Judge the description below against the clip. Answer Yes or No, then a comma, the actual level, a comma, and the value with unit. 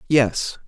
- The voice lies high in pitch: No, low, 135 Hz